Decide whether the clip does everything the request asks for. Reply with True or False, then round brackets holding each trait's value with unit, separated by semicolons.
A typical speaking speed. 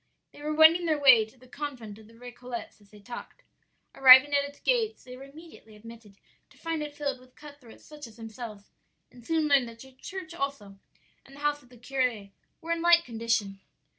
False (210 wpm)